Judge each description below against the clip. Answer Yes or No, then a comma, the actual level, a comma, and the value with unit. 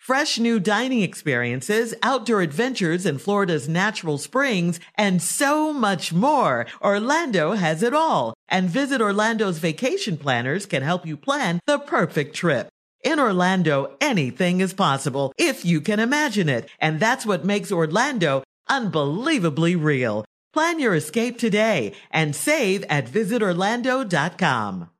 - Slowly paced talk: Yes, slow, 130 wpm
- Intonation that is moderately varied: No, wide, 6.3 semitones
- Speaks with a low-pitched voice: No, high, 200 Hz